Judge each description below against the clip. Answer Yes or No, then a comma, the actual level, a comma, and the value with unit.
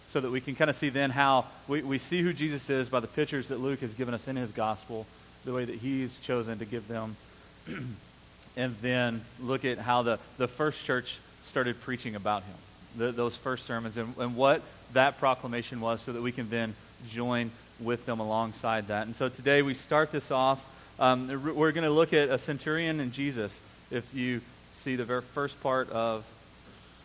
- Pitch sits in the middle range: No, low, 125 Hz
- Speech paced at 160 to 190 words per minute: No, fast, 205 wpm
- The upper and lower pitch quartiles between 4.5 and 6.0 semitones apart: No, average, 2.9 semitones